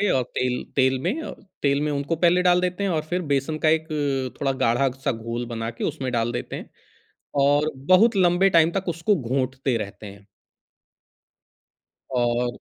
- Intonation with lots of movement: Yes, wide, 6.0 semitones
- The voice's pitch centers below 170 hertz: Yes, medium, 140 Hz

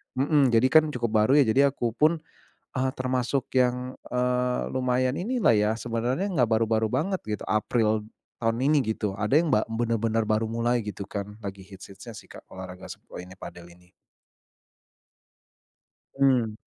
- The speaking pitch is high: No, low, 120 Hz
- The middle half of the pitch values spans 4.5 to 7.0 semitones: No, average, 3.3 semitones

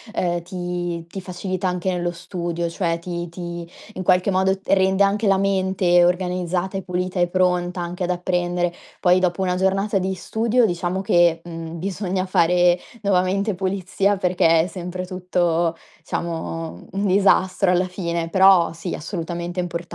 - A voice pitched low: No, medium, 180 Hz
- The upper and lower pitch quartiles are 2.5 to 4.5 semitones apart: No, narrow, 1.6 semitones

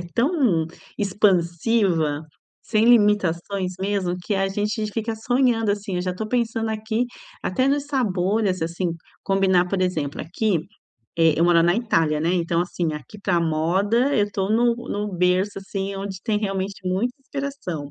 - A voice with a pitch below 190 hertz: No, high, 195 Hz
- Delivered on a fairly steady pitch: No, average, 3.8 semitones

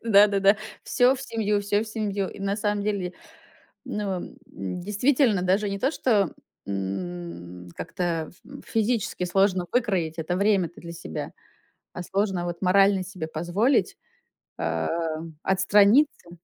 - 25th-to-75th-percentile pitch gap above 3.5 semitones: No, average, 3.2 semitones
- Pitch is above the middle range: Yes, high, 195 Hz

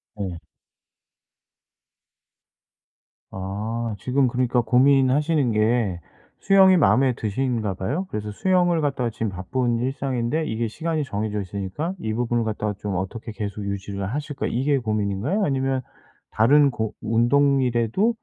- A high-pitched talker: No, low, 120 Hz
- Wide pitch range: No, average, 4.7 semitones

